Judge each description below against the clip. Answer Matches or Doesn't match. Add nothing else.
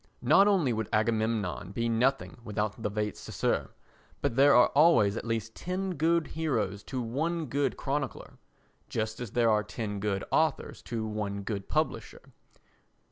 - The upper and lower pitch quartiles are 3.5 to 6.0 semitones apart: Matches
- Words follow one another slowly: Doesn't match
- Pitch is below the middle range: Matches